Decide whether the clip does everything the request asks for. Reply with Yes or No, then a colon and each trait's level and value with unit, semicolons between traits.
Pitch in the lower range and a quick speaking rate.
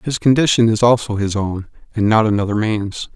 No: low, 110 Hz; average, 190 wpm